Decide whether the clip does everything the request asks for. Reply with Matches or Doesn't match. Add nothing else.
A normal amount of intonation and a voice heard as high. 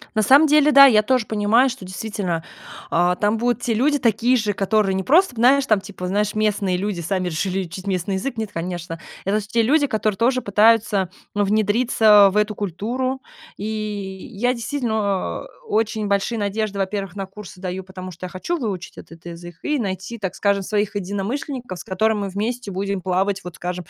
Matches